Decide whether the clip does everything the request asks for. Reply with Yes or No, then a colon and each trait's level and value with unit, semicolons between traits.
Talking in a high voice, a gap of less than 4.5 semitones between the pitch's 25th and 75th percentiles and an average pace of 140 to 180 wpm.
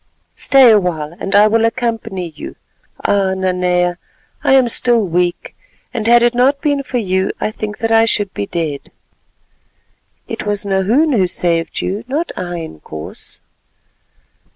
No: high, 205 Hz; average, 4.8 semitones; average, 145 wpm